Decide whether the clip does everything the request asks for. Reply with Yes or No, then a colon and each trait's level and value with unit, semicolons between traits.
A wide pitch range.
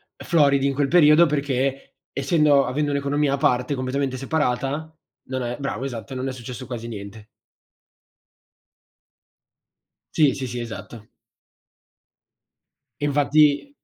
No: narrow, 2.6 semitones